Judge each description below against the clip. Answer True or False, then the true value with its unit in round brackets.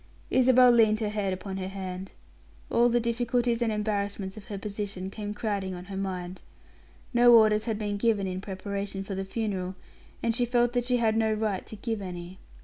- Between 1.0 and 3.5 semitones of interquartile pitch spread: True (3.1 semitones)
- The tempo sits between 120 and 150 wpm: False (195 wpm)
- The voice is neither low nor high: False (210 Hz)